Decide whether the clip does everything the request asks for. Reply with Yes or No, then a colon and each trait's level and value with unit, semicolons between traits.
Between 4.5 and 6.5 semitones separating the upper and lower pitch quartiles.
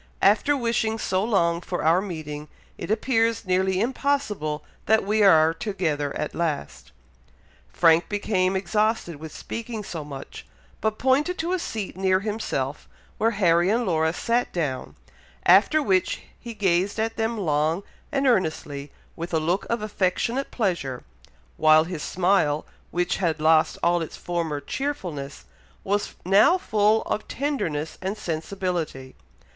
Yes: wide, 5.5 semitones